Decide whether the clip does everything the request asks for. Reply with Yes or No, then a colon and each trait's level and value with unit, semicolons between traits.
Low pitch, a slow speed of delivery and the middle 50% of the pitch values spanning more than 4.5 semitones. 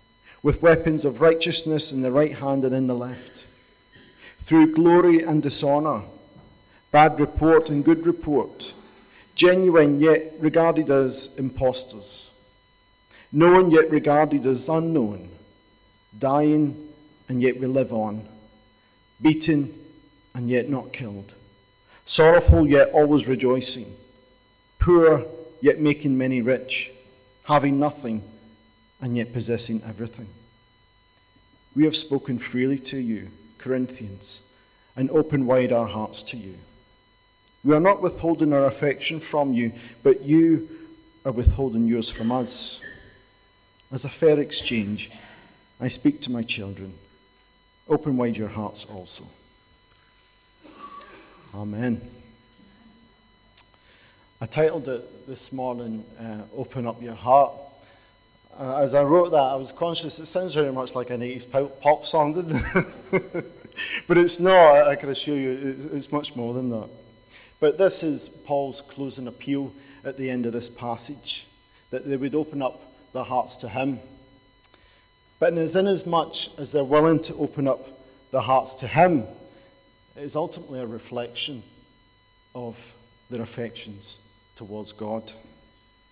Yes: low, 130 Hz; slow, 130 wpm; average, 5.0 semitones